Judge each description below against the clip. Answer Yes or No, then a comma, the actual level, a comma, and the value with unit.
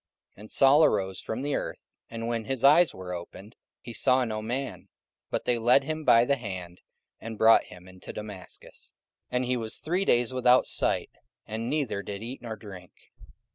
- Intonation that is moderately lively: Yes, average, 4.0 semitones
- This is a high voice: No, low, 115 Hz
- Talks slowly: No, average, 190 wpm